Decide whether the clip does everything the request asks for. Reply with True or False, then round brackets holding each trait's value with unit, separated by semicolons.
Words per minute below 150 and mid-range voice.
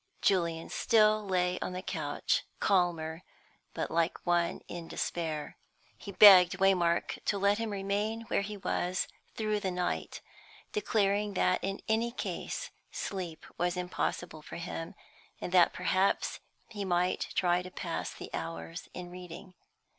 True (140 wpm; 180 Hz)